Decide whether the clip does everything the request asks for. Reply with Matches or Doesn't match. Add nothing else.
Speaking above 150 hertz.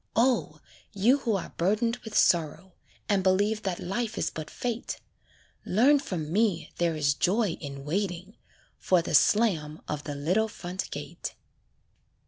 Matches